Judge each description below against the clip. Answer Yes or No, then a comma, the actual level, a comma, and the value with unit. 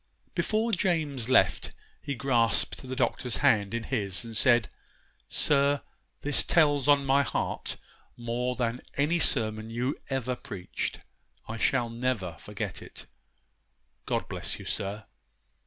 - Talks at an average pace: No, slow, 130 wpm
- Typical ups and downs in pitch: Yes, average, 3.7 semitones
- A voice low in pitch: Yes, low, 125 Hz